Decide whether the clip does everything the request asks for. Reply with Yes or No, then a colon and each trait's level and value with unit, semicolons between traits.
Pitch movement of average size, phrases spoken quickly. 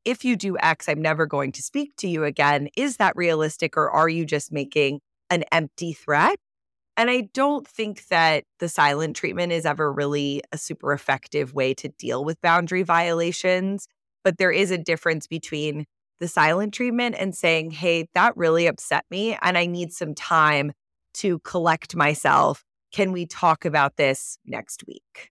No: average, 3.4 semitones; average, 175 wpm